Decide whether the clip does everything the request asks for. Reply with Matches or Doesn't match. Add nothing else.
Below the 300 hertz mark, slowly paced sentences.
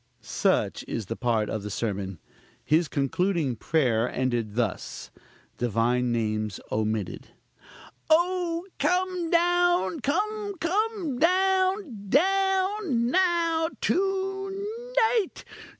Doesn't match